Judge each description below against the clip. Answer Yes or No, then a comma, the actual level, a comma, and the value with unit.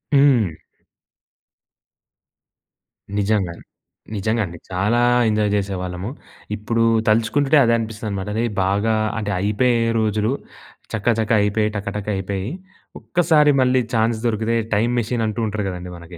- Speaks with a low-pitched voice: Yes, low, 110 Hz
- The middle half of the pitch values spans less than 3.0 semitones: Yes, narrow, 2.6 semitones